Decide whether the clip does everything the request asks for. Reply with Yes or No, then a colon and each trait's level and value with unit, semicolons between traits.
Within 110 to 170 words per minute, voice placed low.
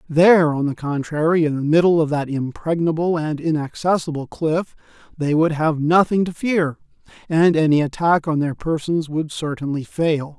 No: average, 160 wpm; medium, 155 Hz